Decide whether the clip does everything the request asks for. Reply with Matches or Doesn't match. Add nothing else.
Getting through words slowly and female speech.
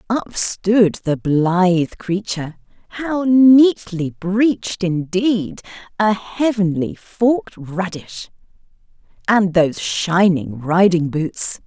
Matches